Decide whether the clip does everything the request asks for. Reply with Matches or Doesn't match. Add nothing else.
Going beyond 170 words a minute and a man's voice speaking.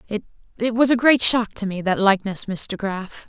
Doesn't match